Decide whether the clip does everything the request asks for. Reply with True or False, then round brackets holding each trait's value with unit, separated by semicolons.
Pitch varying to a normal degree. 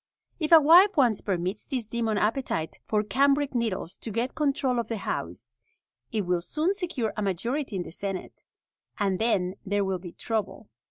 False (5.8 semitones)